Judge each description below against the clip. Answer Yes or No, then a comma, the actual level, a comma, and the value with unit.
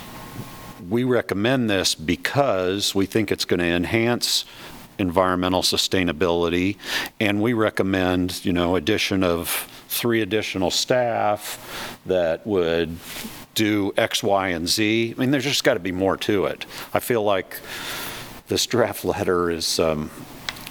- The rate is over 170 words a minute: No, slow, 135 wpm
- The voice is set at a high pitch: No, very low, 95 Hz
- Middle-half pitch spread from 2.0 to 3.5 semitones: No, average, 3.9 semitones